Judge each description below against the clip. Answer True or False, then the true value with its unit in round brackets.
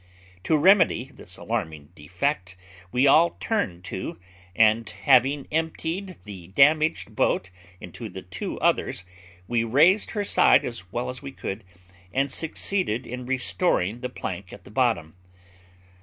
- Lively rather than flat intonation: True (8.1 semitones)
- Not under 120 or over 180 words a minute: True (140 wpm)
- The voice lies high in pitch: False (125 Hz)